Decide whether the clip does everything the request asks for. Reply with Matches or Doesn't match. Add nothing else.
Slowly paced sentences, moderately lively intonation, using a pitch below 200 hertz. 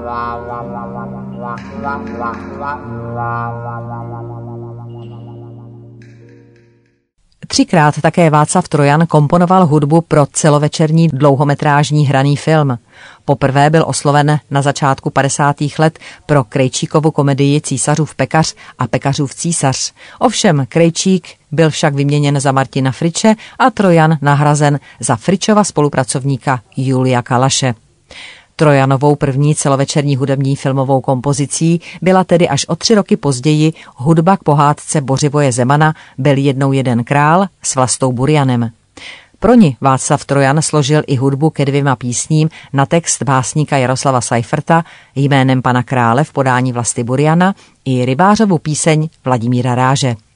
Matches